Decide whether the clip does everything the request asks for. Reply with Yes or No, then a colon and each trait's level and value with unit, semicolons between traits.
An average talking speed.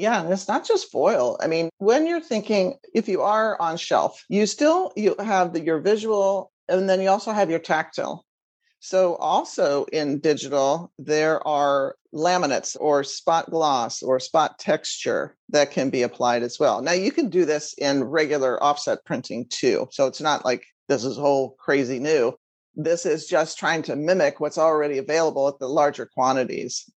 Yes: average, 180 wpm